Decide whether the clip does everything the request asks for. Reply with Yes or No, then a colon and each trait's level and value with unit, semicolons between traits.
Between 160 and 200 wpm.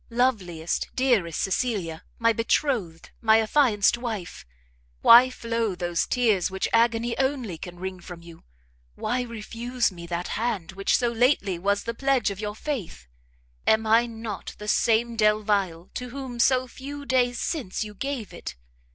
No: average, 150 wpm